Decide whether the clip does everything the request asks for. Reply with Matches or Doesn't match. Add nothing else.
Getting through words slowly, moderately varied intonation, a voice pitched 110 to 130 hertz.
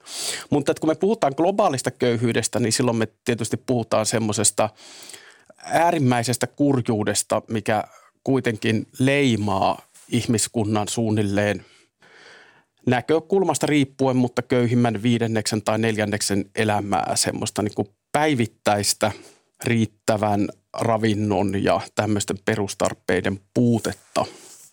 Matches